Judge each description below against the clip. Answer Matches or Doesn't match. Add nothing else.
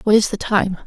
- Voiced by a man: Doesn't match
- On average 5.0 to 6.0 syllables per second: Matches